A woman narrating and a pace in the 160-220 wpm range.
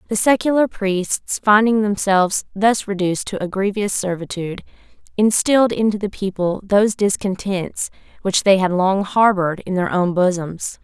No: female; average, 145 wpm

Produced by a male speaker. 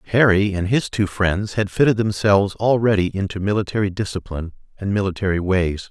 Yes: male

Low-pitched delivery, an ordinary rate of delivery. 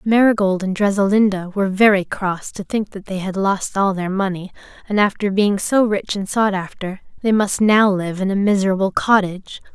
No: high, 195 Hz; average, 190 wpm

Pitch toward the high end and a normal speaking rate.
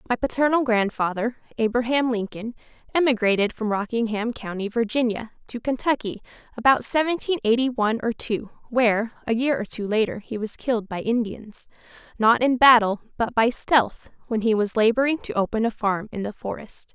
Yes: high, 230 Hz; average, 160 wpm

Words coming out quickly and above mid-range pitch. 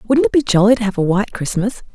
Yes: fast, 280 wpm; high, 210 Hz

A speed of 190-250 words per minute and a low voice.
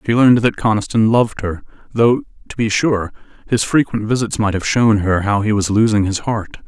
Yes: fast, 205 wpm; low, 110 Hz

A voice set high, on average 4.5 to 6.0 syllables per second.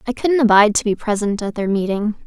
No: high, 220 Hz; 6.4 syllables/s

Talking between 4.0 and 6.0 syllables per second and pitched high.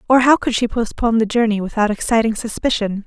No: 6.2 syllables/s; high, 225 Hz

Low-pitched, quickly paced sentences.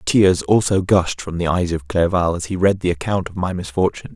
Yes: very low, 90 Hz; fast, 230 wpm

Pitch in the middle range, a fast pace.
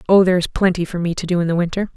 Yes: medium, 175 Hz; fast, 335 wpm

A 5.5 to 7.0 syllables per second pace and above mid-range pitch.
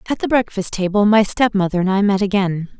Yes: 6.0 syllables/s; high, 200 Hz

